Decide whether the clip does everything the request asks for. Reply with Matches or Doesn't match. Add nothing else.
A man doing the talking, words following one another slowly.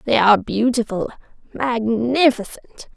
Doesn't match